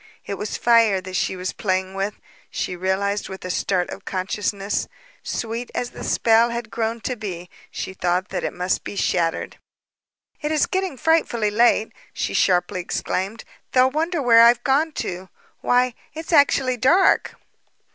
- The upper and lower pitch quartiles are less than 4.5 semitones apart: No, average, 4.8 semitones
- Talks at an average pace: Yes, average, 160 wpm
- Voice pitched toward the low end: No, high, 215 Hz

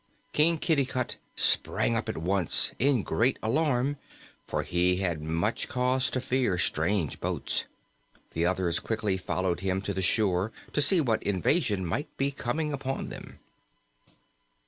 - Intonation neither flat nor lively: No, wide, 6.6 semitones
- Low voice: Yes, low, 110 Hz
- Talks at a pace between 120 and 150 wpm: Yes, average, 145 wpm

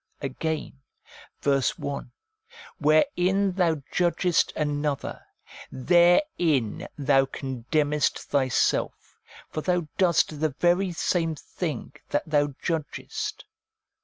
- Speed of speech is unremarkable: No, slow, 100 wpm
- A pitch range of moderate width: Yes, average, 3.6 semitones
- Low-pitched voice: No, medium, 155 Hz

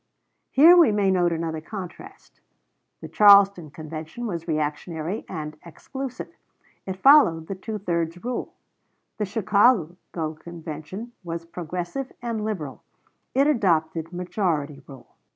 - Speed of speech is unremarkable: No, slow, 115 wpm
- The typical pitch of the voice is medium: Yes, medium, 175 Hz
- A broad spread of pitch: No, average, 4.8 semitones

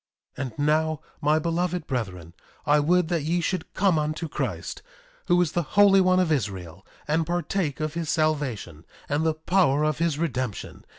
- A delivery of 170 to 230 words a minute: Yes, average, 175 wpm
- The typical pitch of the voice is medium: Yes, medium, 155 Hz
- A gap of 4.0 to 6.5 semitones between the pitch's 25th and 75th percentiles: No, average, 3.4 semitones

